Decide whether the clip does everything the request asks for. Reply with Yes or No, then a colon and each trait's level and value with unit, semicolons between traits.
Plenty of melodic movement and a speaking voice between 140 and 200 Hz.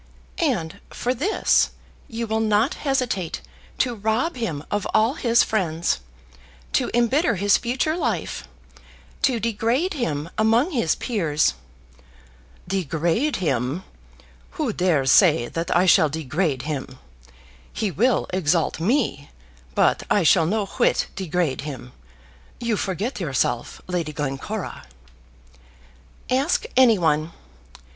Yes: wide, 7.0 semitones; high, 190 Hz